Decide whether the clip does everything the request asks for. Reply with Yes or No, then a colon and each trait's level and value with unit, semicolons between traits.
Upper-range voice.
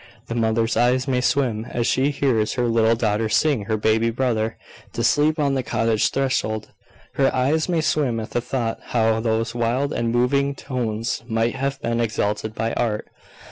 No: low, 120 Hz